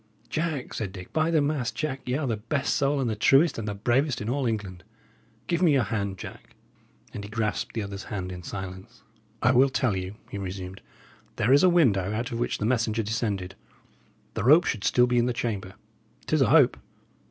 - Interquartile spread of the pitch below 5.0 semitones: No, average, 5.3 semitones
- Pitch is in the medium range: No, low, 115 Hz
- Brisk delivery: Yes, fast, 210 wpm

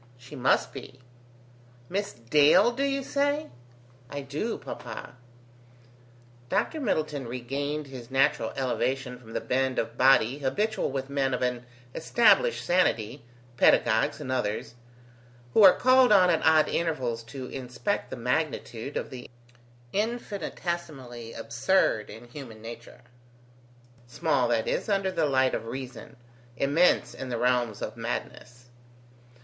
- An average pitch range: No, wide, 5.9 semitones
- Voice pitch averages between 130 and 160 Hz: Yes, low, 135 Hz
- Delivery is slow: Yes, slow, 130 wpm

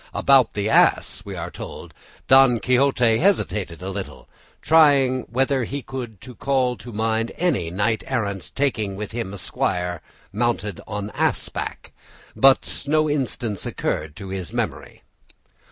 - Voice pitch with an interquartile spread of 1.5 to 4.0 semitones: No, average, 4.8 semitones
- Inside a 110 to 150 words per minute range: Yes, average, 140 wpm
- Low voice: Yes, low, 115 Hz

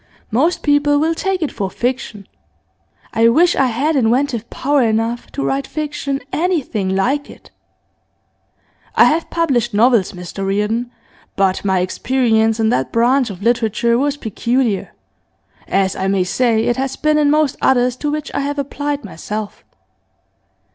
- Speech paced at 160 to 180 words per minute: No, average, 150 wpm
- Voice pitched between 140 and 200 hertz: No, high, 245 Hz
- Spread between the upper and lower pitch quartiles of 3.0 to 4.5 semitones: No, average, 4.9 semitones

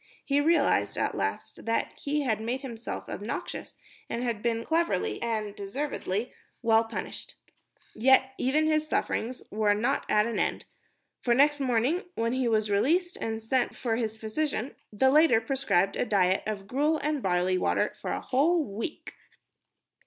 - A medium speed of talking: Yes, average, 160 wpm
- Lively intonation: No, average, 4.7 semitones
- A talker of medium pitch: No, high, 235 Hz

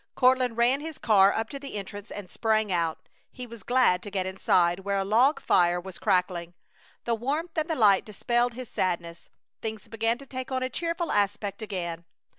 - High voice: Yes, high, 215 Hz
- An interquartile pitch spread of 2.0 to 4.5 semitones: No, average, 5.2 semitones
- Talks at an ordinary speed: Yes, average, 195 wpm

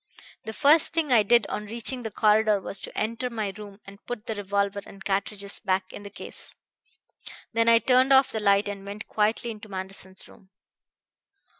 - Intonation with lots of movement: No, narrow, 2.5 semitones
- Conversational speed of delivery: Yes, average, 185 wpm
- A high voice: Yes, high, 210 Hz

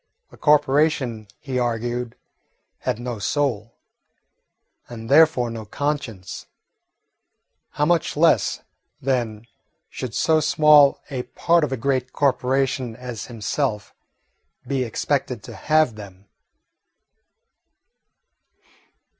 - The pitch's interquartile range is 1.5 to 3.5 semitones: No, average, 4.2 semitones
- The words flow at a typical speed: No, slow, 95 wpm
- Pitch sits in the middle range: No, low, 125 Hz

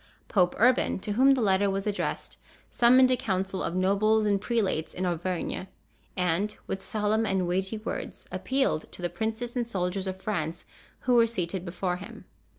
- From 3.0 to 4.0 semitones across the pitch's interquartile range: Yes, average, 3.3 semitones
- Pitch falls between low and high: No, high, 195 Hz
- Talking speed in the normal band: Yes, average, 170 wpm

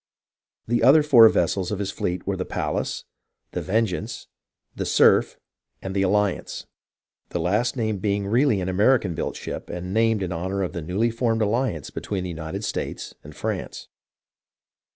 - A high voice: No, low, 100 Hz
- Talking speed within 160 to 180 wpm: Yes, average, 165 wpm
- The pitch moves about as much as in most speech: Yes, average, 3.6 semitones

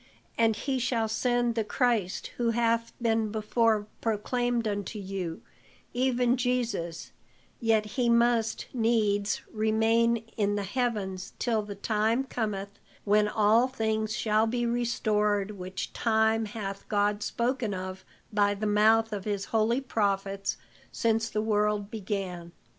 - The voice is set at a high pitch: Yes, high, 220 Hz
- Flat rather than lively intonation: Yes, narrow, 2.2 semitones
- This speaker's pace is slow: Yes, slow, 130 wpm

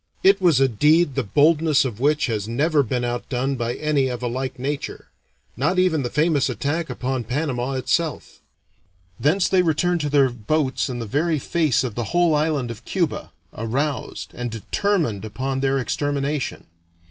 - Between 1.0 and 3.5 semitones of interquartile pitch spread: No, average, 4.1 semitones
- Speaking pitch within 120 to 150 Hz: Yes, medium, 140 Hz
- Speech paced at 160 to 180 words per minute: Yes, average, 170 wpm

